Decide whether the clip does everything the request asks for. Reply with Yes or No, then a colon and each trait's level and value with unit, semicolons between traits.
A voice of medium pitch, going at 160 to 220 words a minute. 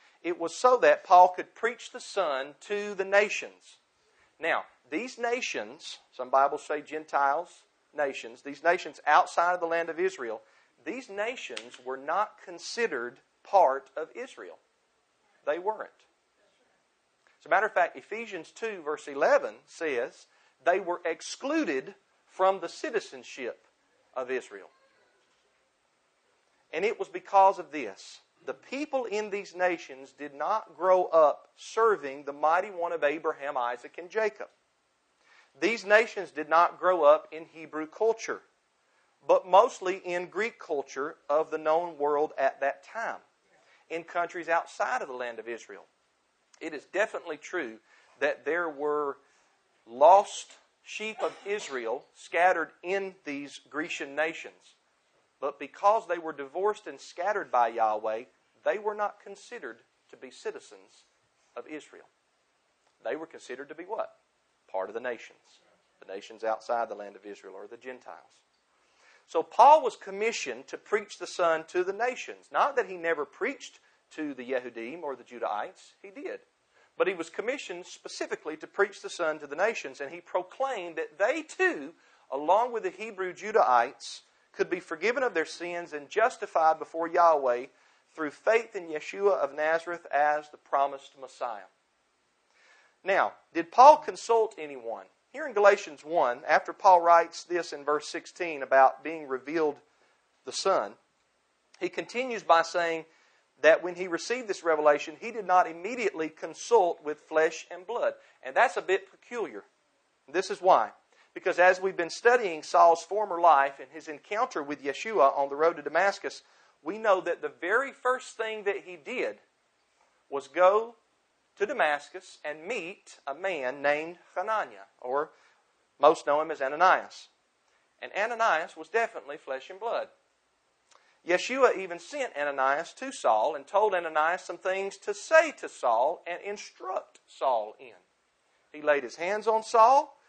No: medium, 175 Hz; average, 150 wpm